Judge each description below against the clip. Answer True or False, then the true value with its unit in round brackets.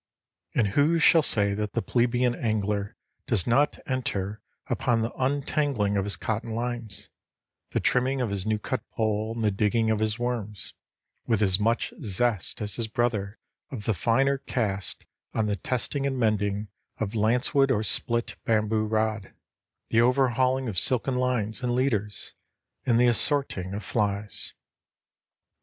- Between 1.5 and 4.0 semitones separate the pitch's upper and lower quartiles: True (3.2 semitones)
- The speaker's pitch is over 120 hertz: False (110 Hz)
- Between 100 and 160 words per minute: True (150 wpm)